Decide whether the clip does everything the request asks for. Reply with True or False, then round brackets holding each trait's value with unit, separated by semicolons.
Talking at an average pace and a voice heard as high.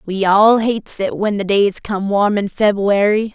True (195 wpm; 205 Hz)